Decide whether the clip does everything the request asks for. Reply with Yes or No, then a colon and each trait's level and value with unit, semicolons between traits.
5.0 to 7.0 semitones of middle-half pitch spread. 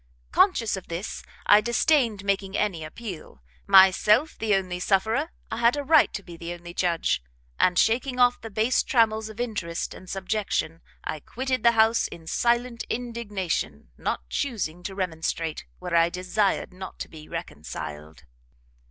Yes: average, 5.3 semitones